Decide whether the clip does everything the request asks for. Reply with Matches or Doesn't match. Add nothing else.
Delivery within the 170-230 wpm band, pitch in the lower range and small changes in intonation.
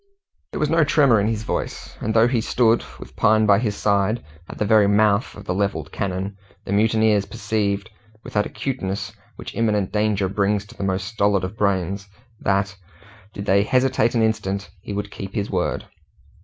Matches